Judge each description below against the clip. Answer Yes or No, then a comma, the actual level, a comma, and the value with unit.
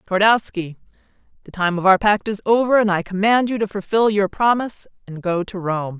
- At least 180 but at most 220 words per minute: Yes, average, 200 wpm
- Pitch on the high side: Yes, high, 200 Hz